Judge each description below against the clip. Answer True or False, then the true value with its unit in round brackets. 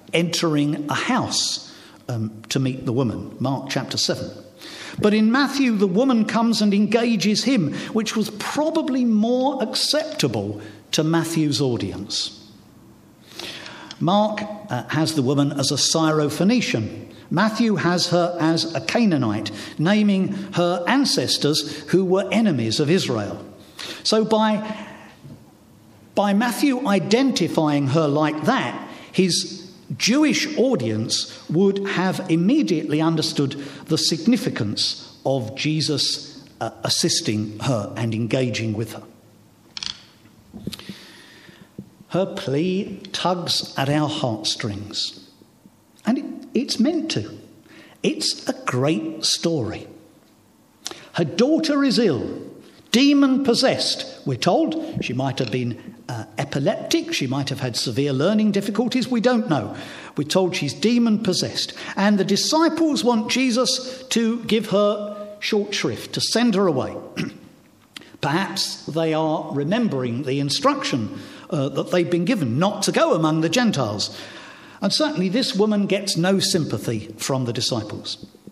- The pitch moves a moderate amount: False (8.1 semitones)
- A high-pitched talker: False (175 Hz)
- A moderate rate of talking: False (120 wpm)